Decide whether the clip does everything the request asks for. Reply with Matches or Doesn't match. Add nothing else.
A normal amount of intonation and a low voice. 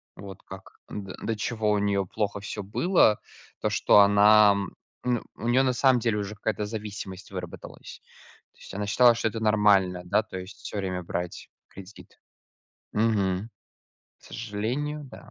Doesn't match